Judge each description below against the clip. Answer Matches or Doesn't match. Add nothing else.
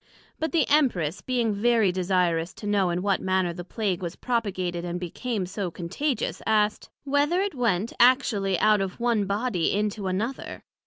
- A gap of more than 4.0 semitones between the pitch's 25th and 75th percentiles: Matches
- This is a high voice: Matches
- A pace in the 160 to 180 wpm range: Matches